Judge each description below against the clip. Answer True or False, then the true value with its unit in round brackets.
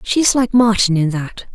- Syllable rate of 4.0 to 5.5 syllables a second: True (4.8 syllables/s)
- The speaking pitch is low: False (210 Hz)